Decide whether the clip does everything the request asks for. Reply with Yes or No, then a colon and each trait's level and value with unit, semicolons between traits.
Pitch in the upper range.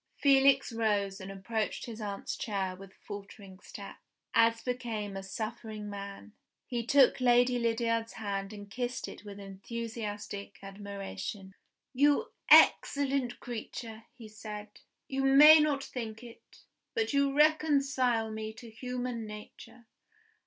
Yes: high, 225 Hz